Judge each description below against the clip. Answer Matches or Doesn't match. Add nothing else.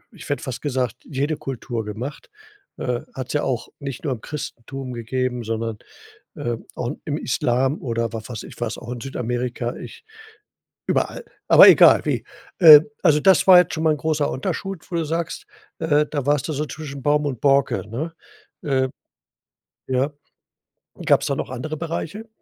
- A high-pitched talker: Doesn't match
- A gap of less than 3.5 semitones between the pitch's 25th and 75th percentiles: Doesn't match